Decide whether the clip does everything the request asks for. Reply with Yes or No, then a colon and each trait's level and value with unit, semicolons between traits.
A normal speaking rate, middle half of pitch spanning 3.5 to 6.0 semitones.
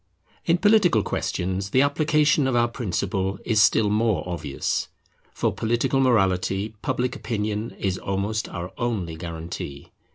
No: slow, 130 wpm; average, 4.7 semitones